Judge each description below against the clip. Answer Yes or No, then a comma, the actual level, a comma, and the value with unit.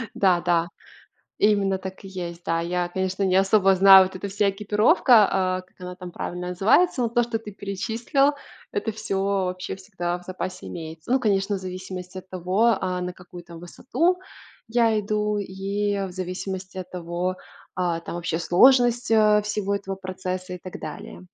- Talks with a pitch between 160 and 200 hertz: Yes, high, 190 Hz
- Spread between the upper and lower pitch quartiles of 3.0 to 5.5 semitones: No, narrow, 2.6 semitones